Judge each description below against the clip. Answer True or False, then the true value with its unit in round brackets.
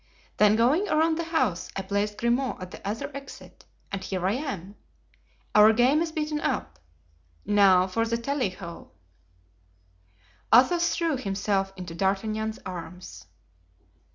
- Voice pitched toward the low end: False (215 Hz)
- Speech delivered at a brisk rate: False (135 wpm)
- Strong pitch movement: True (6.4 semitones)